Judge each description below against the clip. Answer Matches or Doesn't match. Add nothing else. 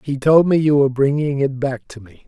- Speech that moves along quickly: Matches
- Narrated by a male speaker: Matches